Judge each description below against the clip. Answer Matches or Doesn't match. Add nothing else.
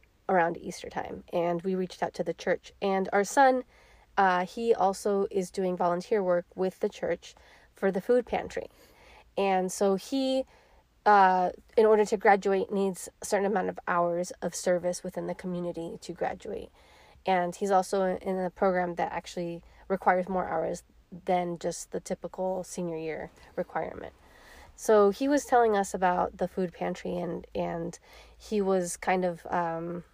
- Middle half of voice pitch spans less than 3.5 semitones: Matches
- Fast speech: Doesn't match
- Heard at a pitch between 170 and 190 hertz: Matches